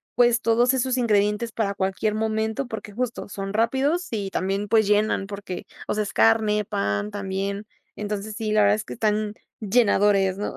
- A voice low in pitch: No, high, 210 Hz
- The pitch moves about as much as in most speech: No, narrow, 2.0 semitones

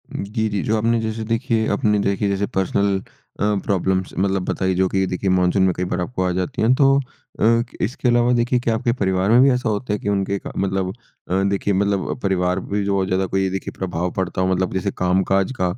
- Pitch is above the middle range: No, low, 100 Hz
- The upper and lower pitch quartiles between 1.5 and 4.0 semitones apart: Yes, average, 2.8 semitones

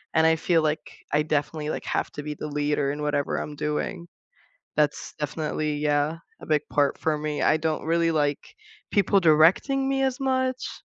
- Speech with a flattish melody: Yes, narrow, 2.1 semitones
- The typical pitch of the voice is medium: Yes, medium, 155 Hz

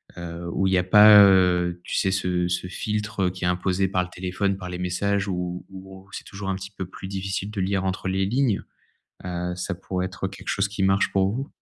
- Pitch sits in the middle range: No, very low, 95 Hz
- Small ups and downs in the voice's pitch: Yes, narrow, 1.5 semitones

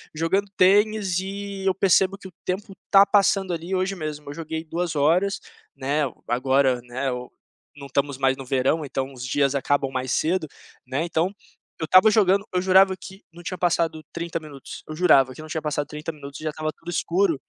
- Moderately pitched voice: Yes, medium, 160 Hz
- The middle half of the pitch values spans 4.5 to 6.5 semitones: Yes, average, 5.1 semitones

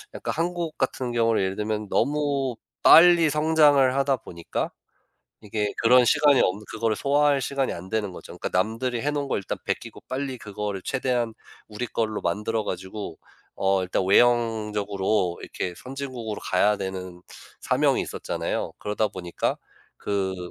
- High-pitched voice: No, low, 110 Hz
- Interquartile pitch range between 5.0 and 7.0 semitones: Yes, wide, 5.4 semitones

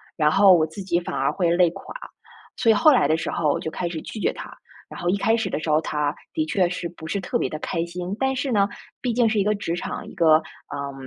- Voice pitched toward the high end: No, medium, 180 Hz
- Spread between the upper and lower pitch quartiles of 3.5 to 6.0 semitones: Yes, average, 4.7 semitones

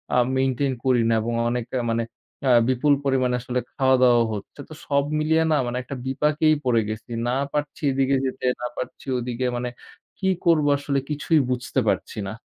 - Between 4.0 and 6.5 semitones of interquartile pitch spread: No, average, 2.8 semitones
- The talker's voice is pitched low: Yes, low, 130 Hz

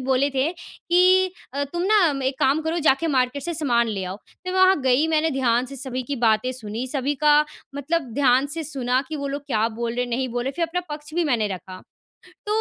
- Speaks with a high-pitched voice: Yes, very high, 270 Hz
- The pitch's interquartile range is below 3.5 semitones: No, average, 4.4 semitones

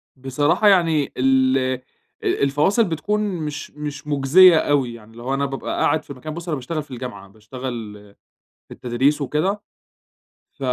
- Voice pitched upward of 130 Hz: Yes, medium, 140 Hz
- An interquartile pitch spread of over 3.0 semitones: Yes, average, 3.4 semitones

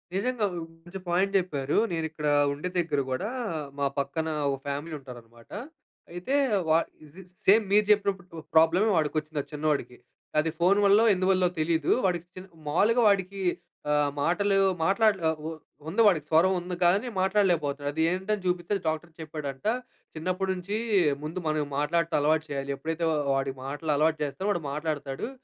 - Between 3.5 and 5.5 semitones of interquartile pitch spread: Yes, average, 4.2 semitones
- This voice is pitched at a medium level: Yes, medium, 165 Hz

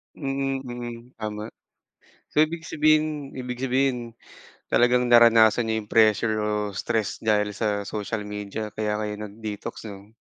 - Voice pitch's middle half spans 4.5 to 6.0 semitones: No, average, 3.1 semitones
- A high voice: No, low, 115 Hz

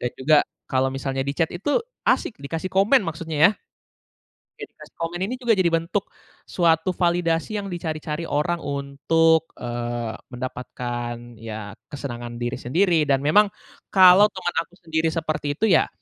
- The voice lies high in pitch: No, medium, 160 Hz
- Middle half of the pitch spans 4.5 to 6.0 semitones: Yes, average, 5.0 semitones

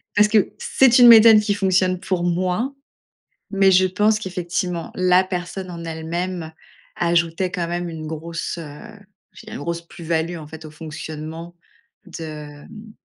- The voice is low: No, medium, 175 Hz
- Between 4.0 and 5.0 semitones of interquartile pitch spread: No, average, 2.9 semitones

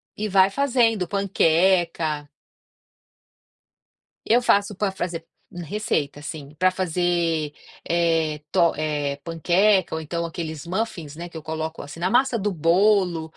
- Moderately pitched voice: Yes, medium, 170 Hz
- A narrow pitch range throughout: No, average, 3.6 semitones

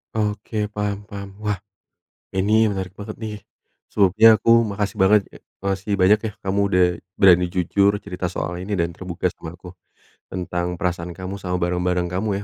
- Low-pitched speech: Yes, very low, 95 Hz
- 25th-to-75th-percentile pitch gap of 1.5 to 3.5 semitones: Yes, narrow, 2.5 semitones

